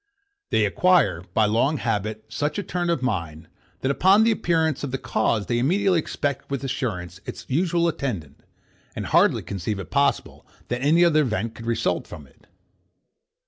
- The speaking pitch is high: No, low, 130 Hz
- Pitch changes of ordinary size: No, wide, 7.2 semitones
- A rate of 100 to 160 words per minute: No, average, 170 wpm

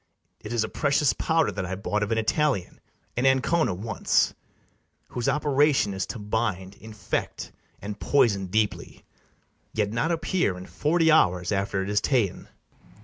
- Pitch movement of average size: No, wide, 6.0 semitones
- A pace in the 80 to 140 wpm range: No, average, 150 wpm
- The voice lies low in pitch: Yes, low, 110 Hz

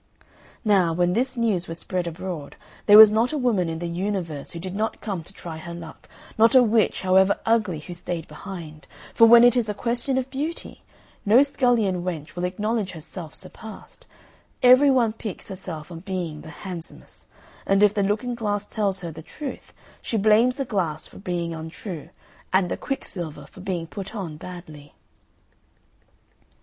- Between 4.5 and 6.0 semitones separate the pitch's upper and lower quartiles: Yes, average, 4.8 semitones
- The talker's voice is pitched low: No, high, 190 Hz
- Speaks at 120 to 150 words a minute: No, average, 175 wpm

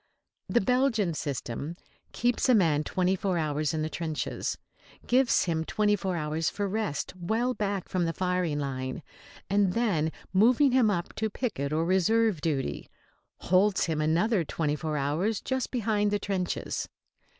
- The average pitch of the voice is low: No, medium, 185 Hz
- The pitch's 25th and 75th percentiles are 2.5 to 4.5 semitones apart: No, wide, 5.5 semitones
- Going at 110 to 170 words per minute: Yes, average, 155 wpm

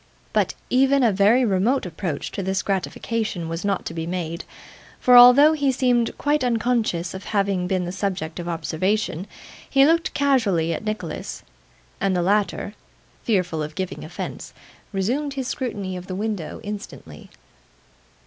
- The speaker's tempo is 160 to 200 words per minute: No, average, 150 wpm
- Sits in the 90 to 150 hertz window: No, high, 200 Hz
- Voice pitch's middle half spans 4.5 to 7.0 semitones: Yes, wide, 5.5 semitones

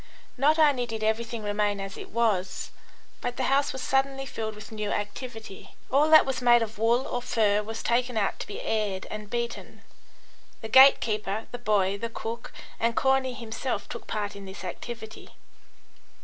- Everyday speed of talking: Yes, average, 175 wpm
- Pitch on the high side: Yes, high, 225 Hz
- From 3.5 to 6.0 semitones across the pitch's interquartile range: No, average, 2.9 semitones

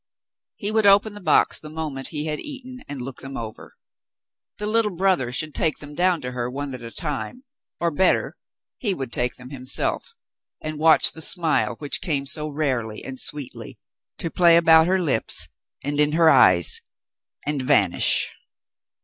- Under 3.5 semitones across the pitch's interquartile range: No, average, 4.6 semitones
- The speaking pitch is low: No, medium, 150 Hz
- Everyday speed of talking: Yes, average, 180 wpm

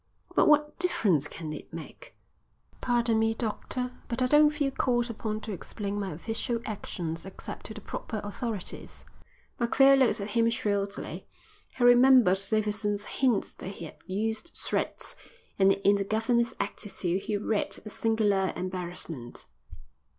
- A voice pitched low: No, high, 215 Hz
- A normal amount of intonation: Yes, average, 3.6 semitones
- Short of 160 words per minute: Yes, average, 145 wpm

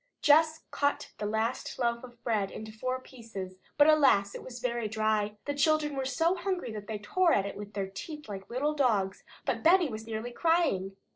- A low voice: No, high, 235 Hz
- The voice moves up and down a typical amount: No, wide, 6.1 semitones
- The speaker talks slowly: No, average, 195 wpm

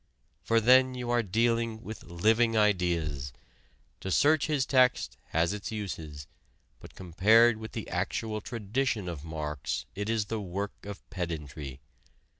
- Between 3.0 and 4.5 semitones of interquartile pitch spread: No, average, 5.2 semitones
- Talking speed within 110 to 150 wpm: Yes, average, 140 wpm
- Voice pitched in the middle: No, low, 105 Hz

